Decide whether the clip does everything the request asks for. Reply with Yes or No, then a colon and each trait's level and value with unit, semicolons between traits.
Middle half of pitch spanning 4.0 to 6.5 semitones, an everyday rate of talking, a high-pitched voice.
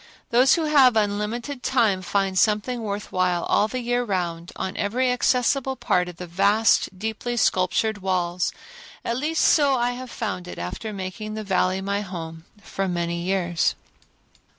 Yes: average, 4.8 semitones; average, 155 wpm; high, 205 Hz